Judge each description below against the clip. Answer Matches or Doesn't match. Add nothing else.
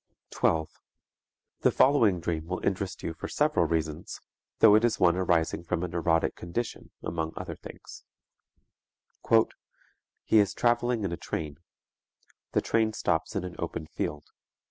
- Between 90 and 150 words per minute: Matches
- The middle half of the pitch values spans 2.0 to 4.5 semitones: Doesn't match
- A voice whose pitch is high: Doesn't match